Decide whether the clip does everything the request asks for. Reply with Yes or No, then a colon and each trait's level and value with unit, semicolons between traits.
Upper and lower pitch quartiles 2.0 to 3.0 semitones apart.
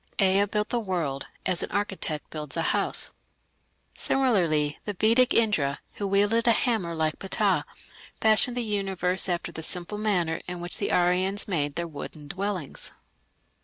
No: average, 4.2 semitones